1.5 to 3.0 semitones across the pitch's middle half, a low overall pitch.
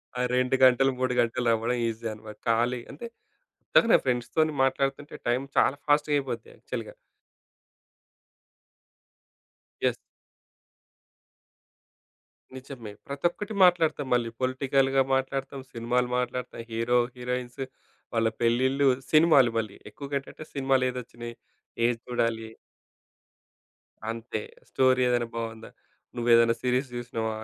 Yes: narrow, 2.6 semitones; low, 125 Hz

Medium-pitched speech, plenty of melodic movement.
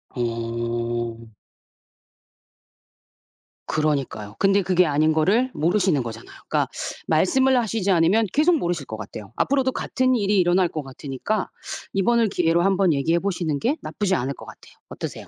Yes: medium, 175 Hz; wide, 7.1 semitones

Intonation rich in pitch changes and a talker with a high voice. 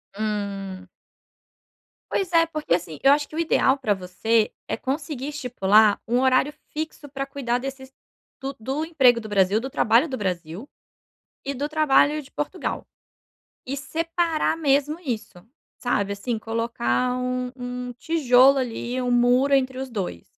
No: average, 4.4 semitones; very high, 255 Hz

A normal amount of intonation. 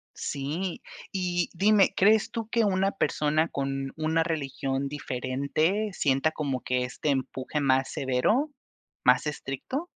No: wide, 5.7 semitones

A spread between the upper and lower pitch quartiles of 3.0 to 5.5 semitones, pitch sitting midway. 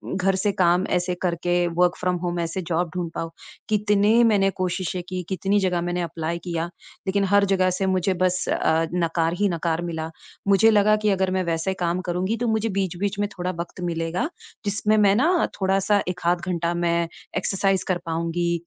No: narrow, 2.4 semitones; medium, 180 Hz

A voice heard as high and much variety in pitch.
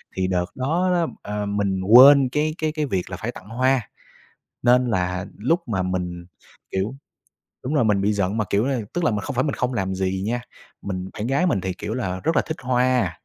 No: low, 110 Hz; wide, 5.8 semitones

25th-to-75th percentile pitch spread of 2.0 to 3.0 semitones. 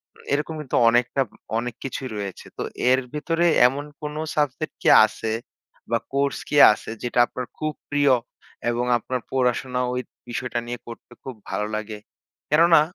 No: average, 3.5 semitones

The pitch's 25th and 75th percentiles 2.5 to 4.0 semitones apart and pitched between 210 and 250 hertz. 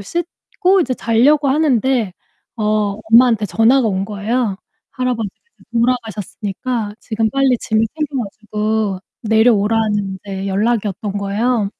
Yes: average, 3.5 semitones; high, 225 Hz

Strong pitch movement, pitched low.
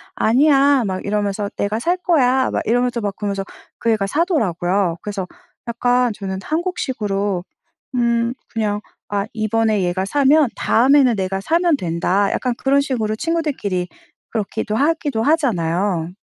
No: wide, 5.7 semitones; high, 225 Hz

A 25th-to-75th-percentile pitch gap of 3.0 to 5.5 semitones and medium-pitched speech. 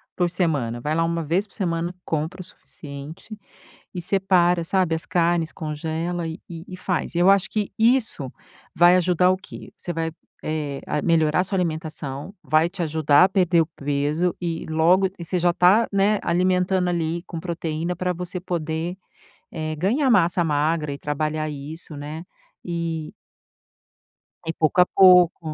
No: narrow, 2.6 semitones; medium, 170 Hz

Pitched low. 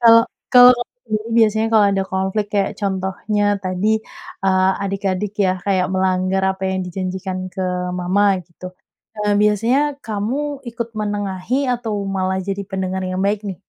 No: high, 195 Hz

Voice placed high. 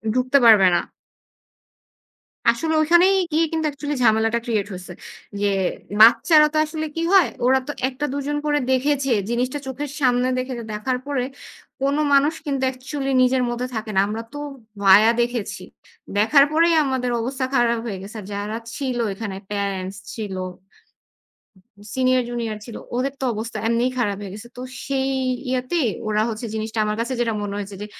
Yes: very high, 250 Hz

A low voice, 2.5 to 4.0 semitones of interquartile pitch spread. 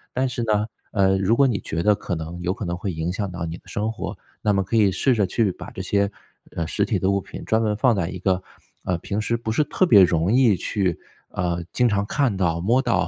Yes: low, 100 Hz; average, 3.5 semitones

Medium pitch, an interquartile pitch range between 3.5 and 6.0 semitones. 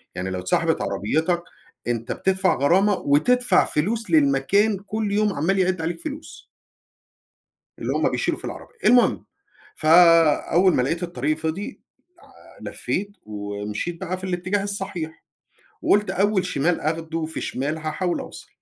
Yes: medium, 175 Hz; average, 4.2 semitones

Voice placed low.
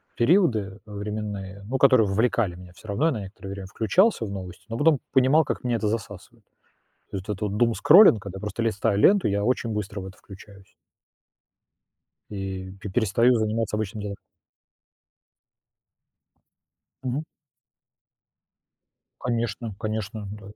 Yes: low, 105 Hz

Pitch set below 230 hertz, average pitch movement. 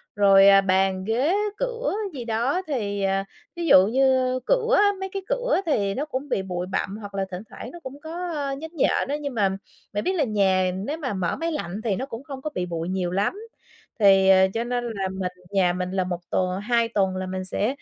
No: high, 215 Hz; wide, 6.8 semitones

